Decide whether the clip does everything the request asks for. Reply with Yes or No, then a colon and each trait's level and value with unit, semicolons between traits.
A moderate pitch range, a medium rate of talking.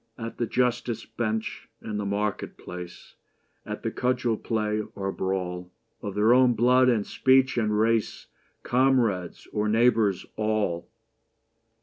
No: average, 3.0 semitones; slow, 130 wpm